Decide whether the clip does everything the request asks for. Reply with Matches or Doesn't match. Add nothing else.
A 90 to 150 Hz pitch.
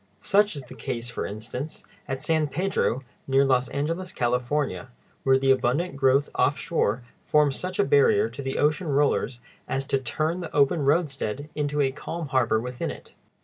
Matches